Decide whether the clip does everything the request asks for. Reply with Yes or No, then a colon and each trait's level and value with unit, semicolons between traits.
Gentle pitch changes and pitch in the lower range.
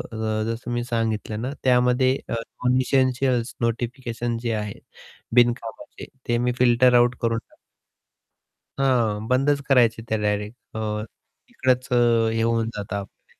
Yes: narrow, 1.9 semitones; low, 120 Hz